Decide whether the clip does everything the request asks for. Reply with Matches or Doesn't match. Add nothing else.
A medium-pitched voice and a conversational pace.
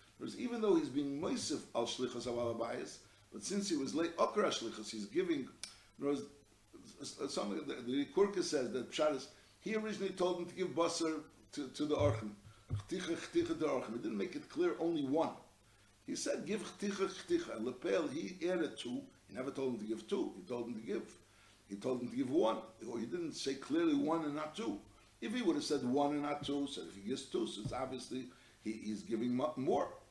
Matches